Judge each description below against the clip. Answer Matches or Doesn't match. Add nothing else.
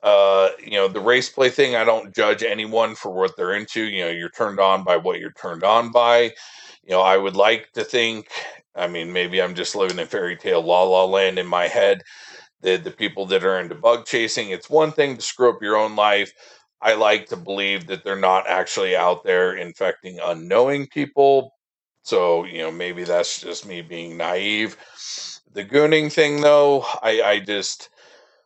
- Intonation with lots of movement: Matches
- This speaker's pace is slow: Doesn't match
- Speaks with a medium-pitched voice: Doesn't match